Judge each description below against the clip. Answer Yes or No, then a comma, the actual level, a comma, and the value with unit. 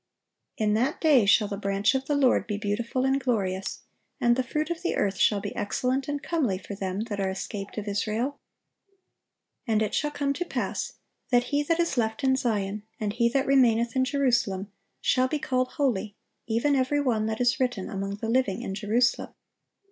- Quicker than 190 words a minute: Yes, average, 200 wpm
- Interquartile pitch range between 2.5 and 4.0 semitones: No, average, 4.4 semitones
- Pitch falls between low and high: No, high, 235 Hz